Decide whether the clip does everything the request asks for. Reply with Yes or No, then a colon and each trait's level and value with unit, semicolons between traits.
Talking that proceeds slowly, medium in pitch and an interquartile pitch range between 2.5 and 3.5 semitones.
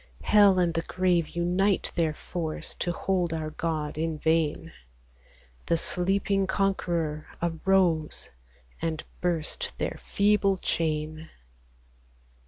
Yes: slow, 110 wpm; medium, 170 Hz; average, 3.1 semitones